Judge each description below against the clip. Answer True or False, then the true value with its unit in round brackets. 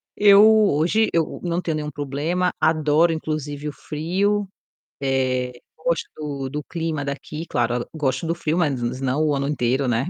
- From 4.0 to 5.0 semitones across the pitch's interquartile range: False (3.2 semitones)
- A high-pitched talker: False (150 Hz)